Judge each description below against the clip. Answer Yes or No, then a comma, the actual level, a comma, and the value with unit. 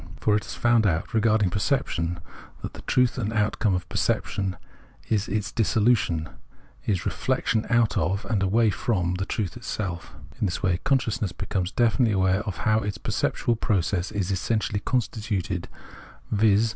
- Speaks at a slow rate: No, average, 160 wpm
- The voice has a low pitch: Yes, low, 105 Hz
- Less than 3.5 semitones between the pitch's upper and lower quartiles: Yes, average, 3.1 semitones